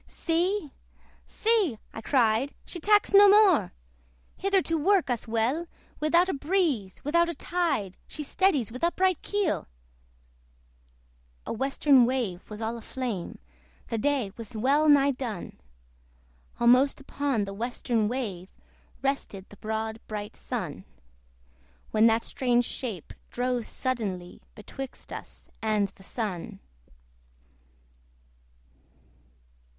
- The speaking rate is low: Yes, slow, 115 wpm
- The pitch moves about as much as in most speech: No, wide, 6.2 semitones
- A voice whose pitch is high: Yes, very high, 255 Hz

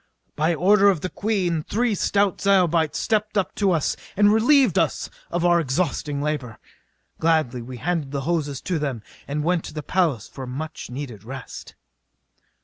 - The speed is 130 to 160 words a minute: No, average, 170 wpm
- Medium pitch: Yes, medium, 165 Hz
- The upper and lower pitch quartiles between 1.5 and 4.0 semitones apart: No, average, 5.3 semitones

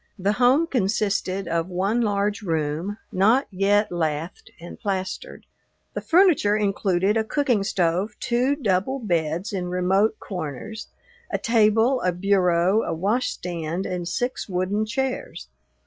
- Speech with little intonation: No, average, 3.8 semitones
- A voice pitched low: No, high, 200 Hz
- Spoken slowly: Yes, slow, 130 wpm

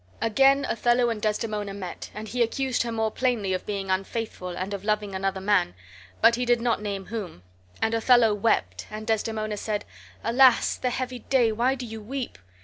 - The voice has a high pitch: Yes, high, 220 Hz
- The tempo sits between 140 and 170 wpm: No, average, 185 wpm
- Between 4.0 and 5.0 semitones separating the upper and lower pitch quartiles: No, average, 2.9 semitones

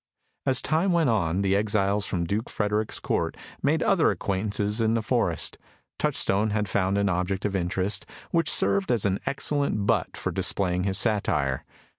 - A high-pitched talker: No, low, 100 Hz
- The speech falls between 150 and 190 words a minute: Yes, average, 165 wpm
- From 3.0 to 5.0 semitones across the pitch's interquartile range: No, narrow, 2.4 semitones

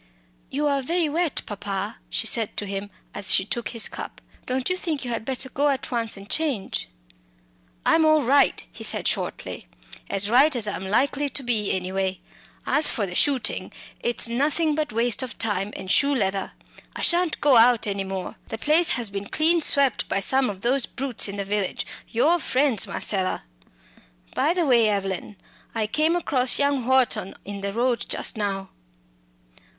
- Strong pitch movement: Yes, wide, 5.9 semitones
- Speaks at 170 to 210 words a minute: Yes, average, 180 wpm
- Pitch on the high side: Yes, high, 240 Hz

